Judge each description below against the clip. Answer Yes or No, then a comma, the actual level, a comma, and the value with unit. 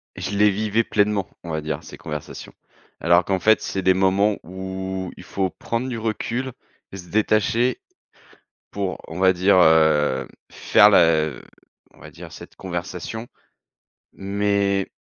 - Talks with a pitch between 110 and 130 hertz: No, very low, 95 Hz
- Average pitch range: Yes, average, 3.0 semitones